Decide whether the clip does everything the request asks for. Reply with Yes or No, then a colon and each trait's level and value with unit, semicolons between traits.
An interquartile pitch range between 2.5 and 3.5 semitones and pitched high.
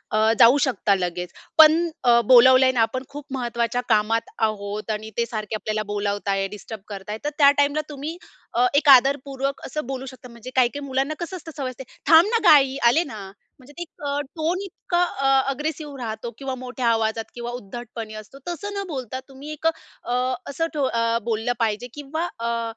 No: average, 4.2 semitones; very high, 255 Hz